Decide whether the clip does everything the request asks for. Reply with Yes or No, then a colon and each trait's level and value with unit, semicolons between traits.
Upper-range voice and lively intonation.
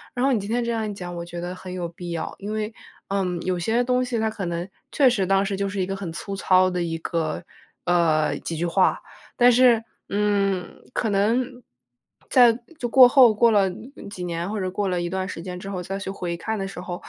No: high, 195 Hz; average, 3.7 semitones